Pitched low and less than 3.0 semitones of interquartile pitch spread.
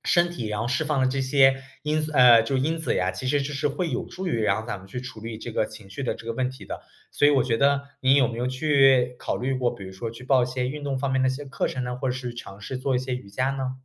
Yes: low, 130 Hz; narrow, 2.4 semitones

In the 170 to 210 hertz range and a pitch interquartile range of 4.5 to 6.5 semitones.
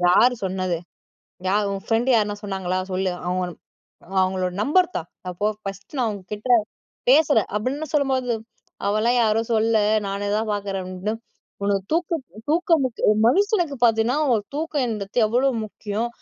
No: high, 220 Hz; average, 4.8 semitones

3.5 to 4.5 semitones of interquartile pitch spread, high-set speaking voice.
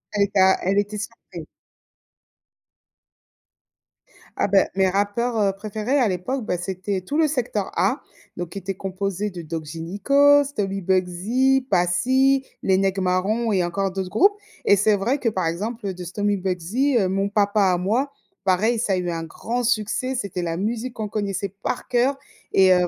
Yes: average, 4.2 semitones; high, 200 Hz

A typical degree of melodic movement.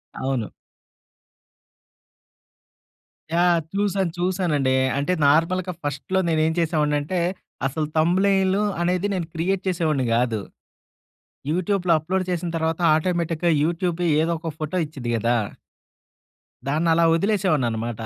Yes: average, 3.4 semitones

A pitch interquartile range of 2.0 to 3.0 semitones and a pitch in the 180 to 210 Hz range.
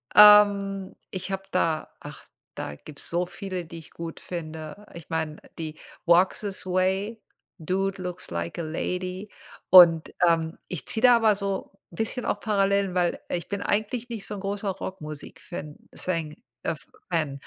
No: average, 3.5 semitones; medium, 185 Hz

